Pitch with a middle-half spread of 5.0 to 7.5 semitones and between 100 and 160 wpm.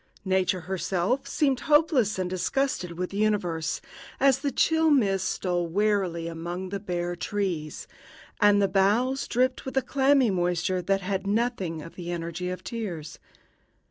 Yes: wide, 5.4 semitones; average, 150 wpm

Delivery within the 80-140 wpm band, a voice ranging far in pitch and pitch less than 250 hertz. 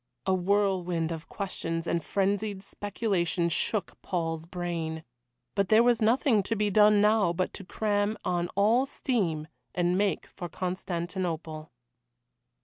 No: slow, 135 wpm; average, 3.4 semitones; high, 190 Hz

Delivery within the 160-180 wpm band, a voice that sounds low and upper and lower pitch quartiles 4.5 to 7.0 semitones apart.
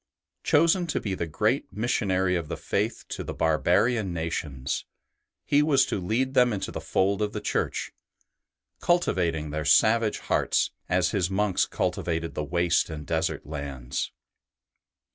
No: average, 145 wpm; very low, 90 Hz; average, 5.2 semitones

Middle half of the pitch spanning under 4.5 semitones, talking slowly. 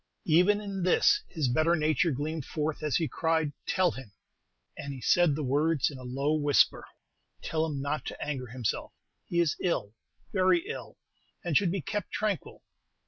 No: average, 3.6 semitones; average, 175 wpm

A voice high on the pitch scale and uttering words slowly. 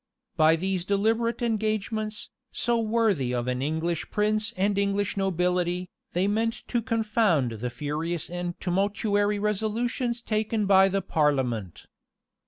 Yes: high, 200 Hz; slow, 130 wpm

